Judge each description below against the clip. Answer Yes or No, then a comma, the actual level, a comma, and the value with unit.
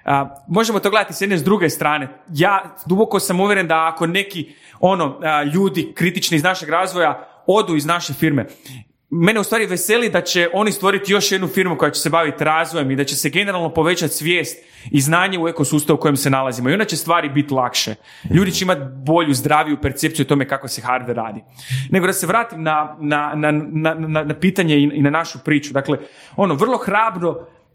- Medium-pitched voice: Yes, medium, 160 Hz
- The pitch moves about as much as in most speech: Yes, average, 4.1 semitones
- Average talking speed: No, fast, 210 wpm